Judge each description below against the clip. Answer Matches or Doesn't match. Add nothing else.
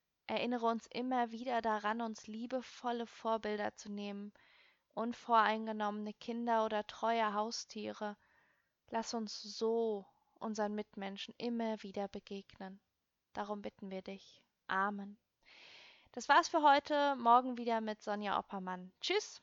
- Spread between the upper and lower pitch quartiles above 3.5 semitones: Doesn't match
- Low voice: Doesn't match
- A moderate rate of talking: Doesn't match